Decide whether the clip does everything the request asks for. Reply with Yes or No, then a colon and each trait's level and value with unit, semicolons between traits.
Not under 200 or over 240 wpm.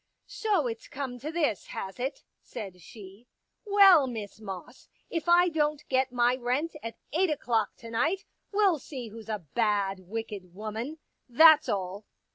No: average, 175 wpm